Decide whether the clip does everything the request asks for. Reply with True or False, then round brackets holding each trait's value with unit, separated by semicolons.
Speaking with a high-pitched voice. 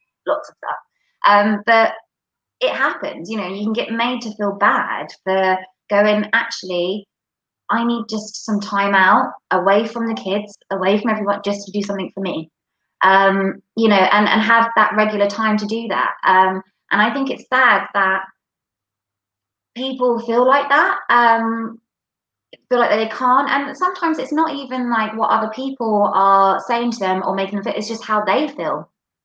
True (210 Hz)